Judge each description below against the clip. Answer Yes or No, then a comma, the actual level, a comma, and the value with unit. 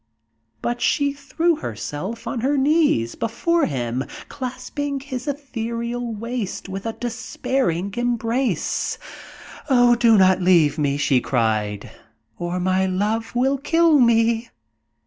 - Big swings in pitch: Yes, wide, 6.2 semitones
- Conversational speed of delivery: No, slow, 120 wpm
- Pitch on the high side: Yes, high, 230 Hz